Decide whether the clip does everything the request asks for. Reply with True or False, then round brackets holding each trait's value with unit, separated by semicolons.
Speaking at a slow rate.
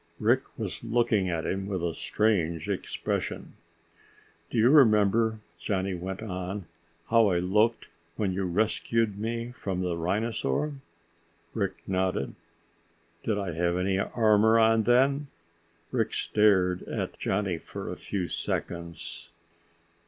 True (125 wpm)